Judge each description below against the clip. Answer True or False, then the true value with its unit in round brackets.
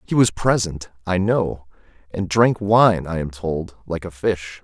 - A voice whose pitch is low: True (95 Hz)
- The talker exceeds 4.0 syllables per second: False (3.9 syllables/s)